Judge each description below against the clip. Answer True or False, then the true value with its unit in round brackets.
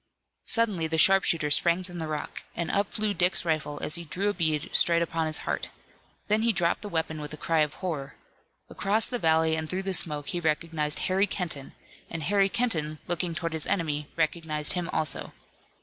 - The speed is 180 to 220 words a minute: True (195 wpm)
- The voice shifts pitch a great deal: False (3.3 semitones)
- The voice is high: False (165 Hz)